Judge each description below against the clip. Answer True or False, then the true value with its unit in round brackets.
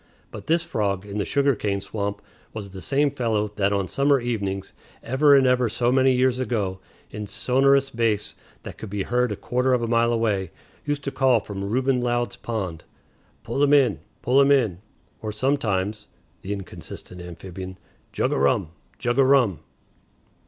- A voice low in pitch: True (115 Hz)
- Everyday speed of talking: True (175 wpm)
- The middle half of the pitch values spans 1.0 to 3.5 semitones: False (4.8 semitones)